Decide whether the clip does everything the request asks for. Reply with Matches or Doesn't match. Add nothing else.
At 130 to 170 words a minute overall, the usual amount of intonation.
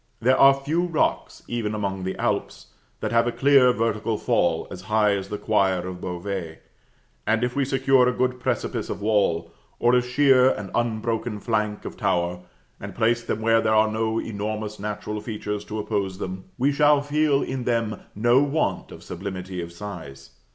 Doesn't match